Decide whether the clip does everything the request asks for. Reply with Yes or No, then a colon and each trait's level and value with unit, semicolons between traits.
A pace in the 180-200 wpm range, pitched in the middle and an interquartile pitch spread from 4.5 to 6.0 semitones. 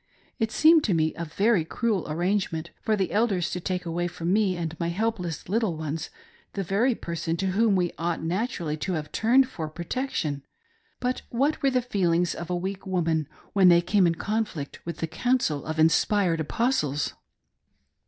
Yes: average, 185 wpm; medium, 180 Hz; average, 4.9 semitones